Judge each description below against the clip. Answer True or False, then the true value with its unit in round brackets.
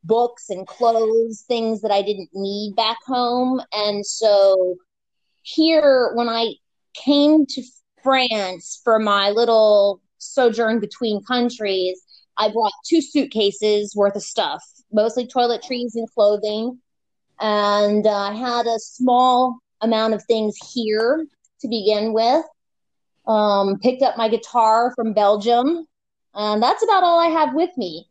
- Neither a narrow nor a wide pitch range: True (3.2 semitones)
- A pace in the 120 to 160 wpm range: True (135 wpm)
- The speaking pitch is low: False (225 Hz)